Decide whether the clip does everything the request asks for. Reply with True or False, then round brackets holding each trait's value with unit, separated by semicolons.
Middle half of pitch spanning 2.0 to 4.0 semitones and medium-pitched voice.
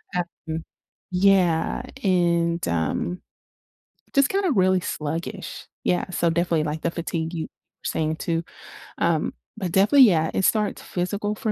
True (2.9 semitones; 175 Hz)